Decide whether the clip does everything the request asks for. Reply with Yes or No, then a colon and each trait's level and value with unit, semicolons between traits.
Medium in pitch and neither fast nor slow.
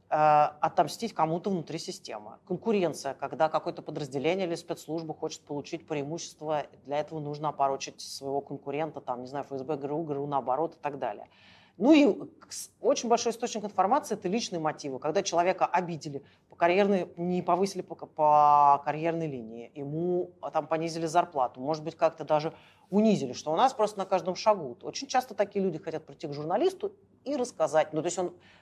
No: medium, 160 Hz; fast, 170 wpm